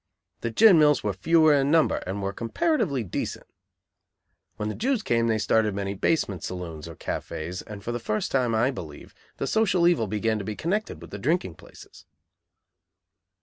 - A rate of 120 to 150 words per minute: No, average, 180 wpm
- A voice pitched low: Yes, low, 115 Hz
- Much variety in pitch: Yes, wide, 7.9 semitones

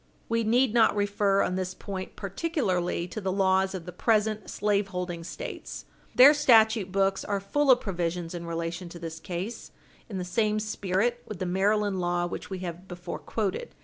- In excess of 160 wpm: Yes, average, 180 wpm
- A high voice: Yes, high, 195 Hz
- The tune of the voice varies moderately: Yes, average, 3.2 semitones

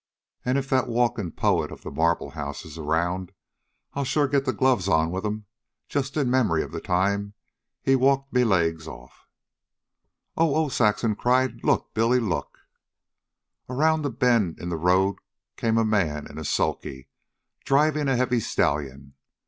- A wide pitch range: Yes, wide, 7.2 semitones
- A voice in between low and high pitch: No, low, 110 Hz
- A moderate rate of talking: Yes, average, 170 wpm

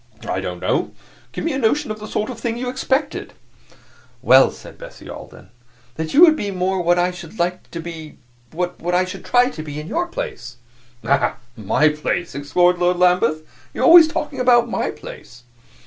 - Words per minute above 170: Yes, average, 195 wpm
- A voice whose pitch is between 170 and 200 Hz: Yes, medium, 185 Hz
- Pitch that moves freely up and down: Yes, wide, 7.4 semitones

